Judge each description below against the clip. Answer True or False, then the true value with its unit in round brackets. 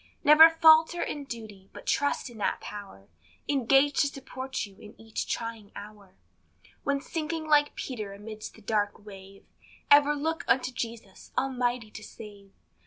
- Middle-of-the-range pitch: False (235 Hz)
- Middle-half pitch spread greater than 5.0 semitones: True (5.6 semitones)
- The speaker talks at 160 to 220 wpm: False (150 wpm)